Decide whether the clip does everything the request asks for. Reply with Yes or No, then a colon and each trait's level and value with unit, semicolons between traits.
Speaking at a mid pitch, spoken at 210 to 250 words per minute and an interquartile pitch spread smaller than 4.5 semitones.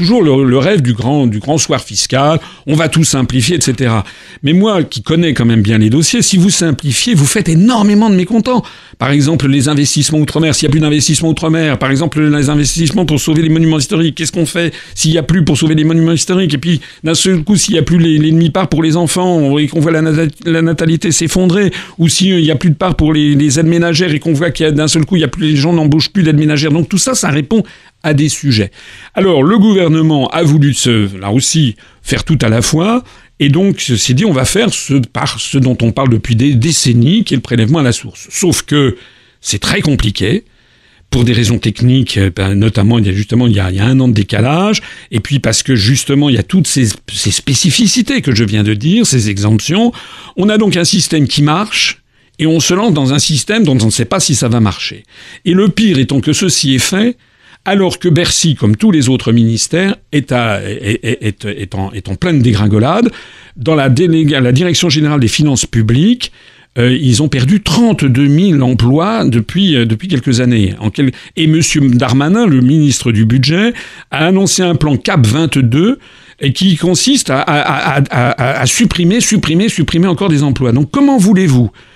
No: medium, 150 Hz; fast, 220 wpm; average, 5.3 semitones